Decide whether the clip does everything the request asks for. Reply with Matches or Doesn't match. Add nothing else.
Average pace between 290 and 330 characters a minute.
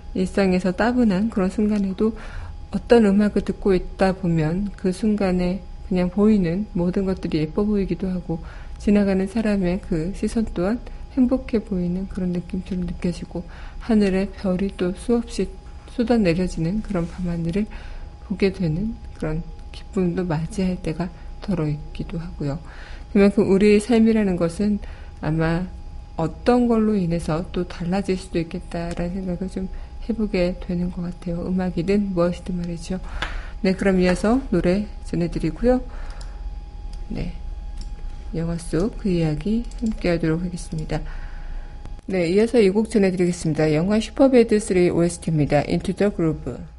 Matches